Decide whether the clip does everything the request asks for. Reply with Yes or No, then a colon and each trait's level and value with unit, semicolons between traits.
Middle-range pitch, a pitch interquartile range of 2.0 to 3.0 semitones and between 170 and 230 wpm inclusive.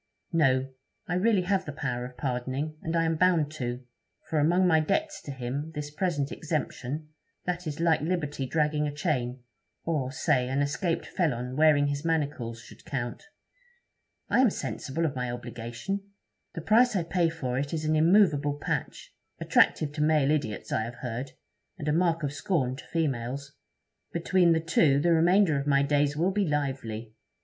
No: medium, 150 Hz; average, 3.8 semitones; average, 175 wpm